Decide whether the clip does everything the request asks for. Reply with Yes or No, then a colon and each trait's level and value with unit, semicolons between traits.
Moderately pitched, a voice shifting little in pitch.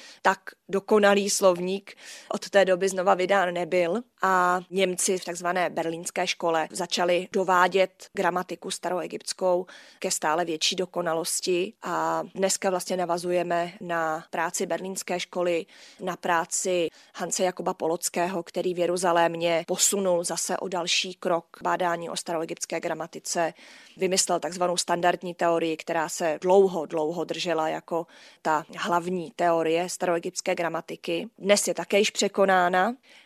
Yes: medium, 180 Hz; narrow, 1.9 semitones